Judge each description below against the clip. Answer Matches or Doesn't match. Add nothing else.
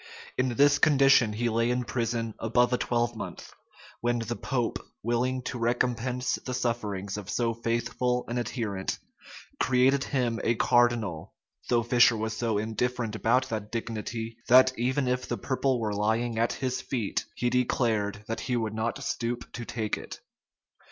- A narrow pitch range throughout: Matches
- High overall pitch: Doesn't match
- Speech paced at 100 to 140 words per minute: Doesn't match